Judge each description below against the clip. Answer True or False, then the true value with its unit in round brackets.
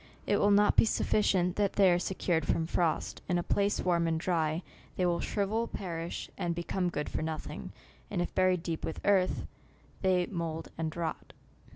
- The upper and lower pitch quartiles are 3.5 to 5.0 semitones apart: False (2.6 semitones)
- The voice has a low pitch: False (175 Hz)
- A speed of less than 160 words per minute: False (185 wpm)